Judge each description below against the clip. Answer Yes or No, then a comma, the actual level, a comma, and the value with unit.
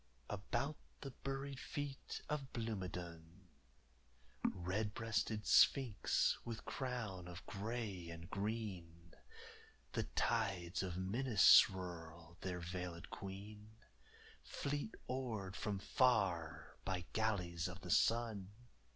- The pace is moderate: No, slow, 100 wpm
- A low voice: Yes, low, 100 Hz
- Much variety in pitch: No, average, 4.6 semitones